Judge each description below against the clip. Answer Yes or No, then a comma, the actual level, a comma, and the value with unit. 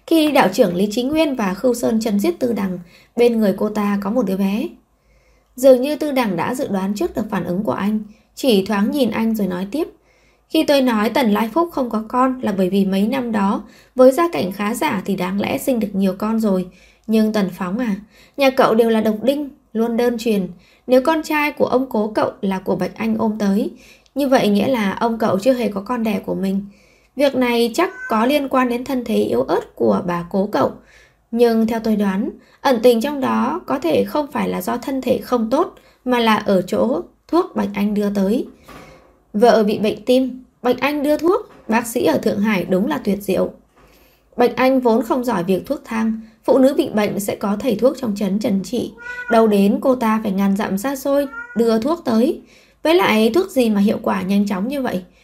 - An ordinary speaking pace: Yes, average, 230 wpm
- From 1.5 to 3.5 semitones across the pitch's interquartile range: No, average, 4.3 semitones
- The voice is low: No, high, 230 Hz